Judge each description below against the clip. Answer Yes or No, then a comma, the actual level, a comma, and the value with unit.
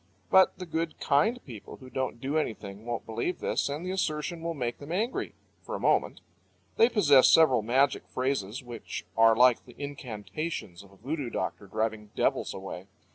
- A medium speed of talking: Yes, average, 180 wpm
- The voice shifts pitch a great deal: Yes, wide, 6.1 semitones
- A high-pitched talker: No, low, 130 Hz